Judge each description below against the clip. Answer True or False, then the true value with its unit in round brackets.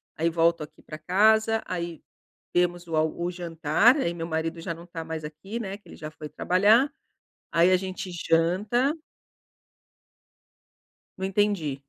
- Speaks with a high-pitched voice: False (175 Hz)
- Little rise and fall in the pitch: False (3.2 semitones)